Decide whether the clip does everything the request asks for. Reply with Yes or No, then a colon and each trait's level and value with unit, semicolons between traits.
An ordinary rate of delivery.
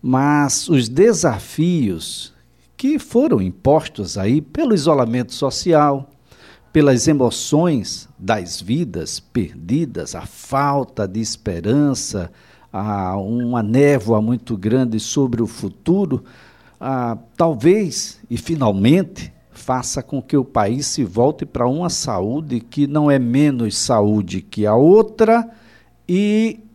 No: slow, 110 wpm